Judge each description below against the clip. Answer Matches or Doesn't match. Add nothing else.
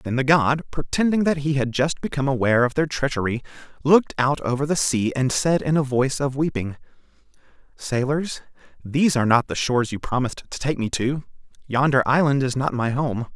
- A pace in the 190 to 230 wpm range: Matches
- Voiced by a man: Matches